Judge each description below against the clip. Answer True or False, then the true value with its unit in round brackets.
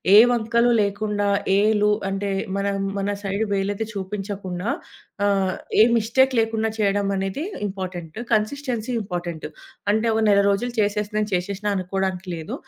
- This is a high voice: True (200 Hz)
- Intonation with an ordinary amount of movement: False (2.1 semitones)